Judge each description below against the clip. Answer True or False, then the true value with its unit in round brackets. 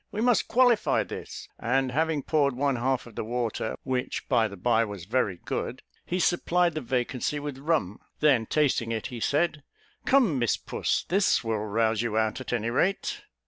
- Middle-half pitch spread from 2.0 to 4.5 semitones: False (5.3 semitones)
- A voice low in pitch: True (130 Hz)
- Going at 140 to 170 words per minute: False (185 wpm)